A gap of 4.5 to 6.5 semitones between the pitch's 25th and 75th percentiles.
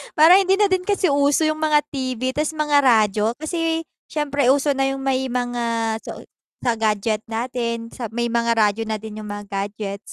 Yes: average, 5.0 semitones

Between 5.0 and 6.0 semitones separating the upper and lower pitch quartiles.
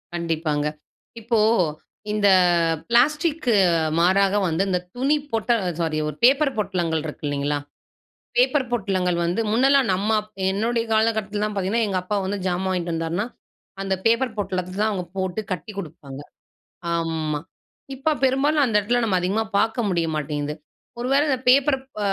Yes: wide, 5.6 semitones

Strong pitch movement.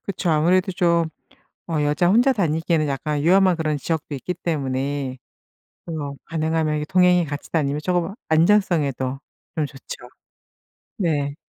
No: average, 3.4 semitones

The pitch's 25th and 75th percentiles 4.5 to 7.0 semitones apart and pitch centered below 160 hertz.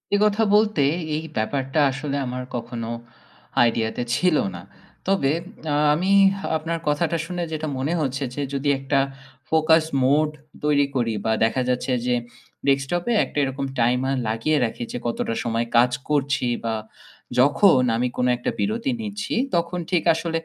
Yes: average, 4.8 semitones; medium, 140 Hz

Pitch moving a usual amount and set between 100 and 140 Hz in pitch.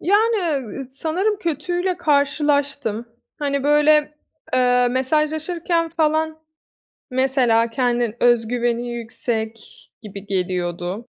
No: average, 5.0 semitones; very high, 265 Hz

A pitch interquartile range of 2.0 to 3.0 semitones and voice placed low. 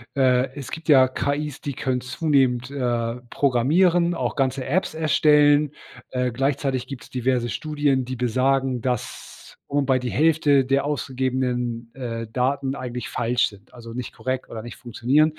Yes: narrow, 2.5 semitones; low, 130 Hz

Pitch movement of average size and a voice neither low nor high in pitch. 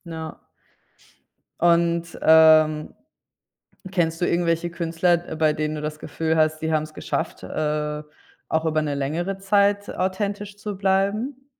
Yes: average, 3.6 semitones; medium, 165 Hz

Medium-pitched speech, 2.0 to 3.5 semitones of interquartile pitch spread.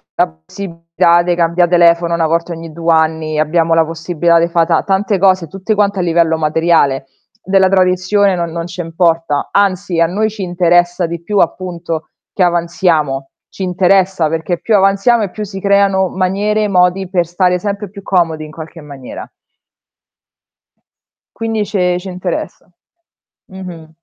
Yes: medium, 175 Hz; narrow, 2.5 semitones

